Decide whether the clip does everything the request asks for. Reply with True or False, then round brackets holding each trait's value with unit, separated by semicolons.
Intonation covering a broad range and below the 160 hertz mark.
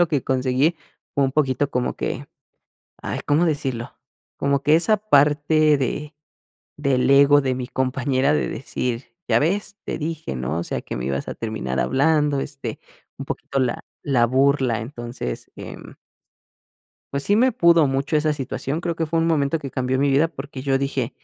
False (2.9 semitones; 140 Hz)